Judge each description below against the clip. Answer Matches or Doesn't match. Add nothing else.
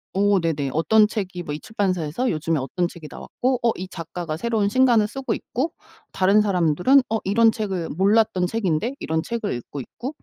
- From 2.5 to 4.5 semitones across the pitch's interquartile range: Doesn't match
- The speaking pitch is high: Matches